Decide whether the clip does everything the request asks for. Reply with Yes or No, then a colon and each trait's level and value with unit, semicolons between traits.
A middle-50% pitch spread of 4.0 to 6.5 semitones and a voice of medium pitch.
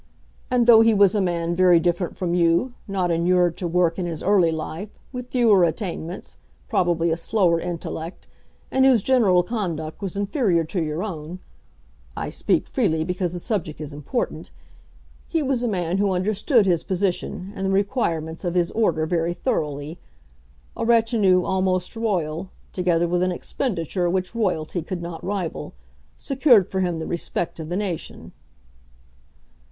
No: average, 3.4 semitones; medium, 180 Hz